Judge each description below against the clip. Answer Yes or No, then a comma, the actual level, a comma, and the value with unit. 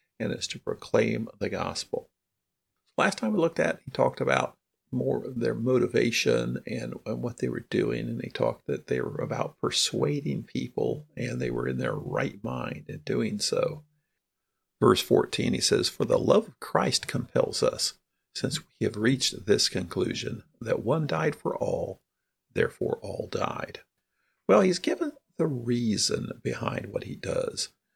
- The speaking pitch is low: No, medium, 180 Hz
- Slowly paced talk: No, average, 165 wpm